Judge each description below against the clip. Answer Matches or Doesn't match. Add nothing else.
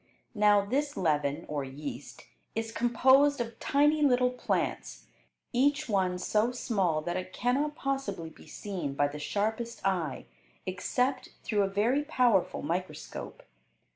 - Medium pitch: Doesn't match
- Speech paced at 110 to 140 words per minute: Matches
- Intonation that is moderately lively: Doesn't match